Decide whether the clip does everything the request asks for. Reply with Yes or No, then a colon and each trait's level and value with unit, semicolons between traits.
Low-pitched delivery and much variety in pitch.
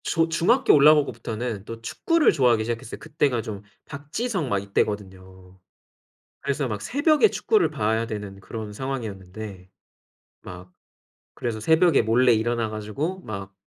Yes: low, 115 Hz; wide, 6.1 semitones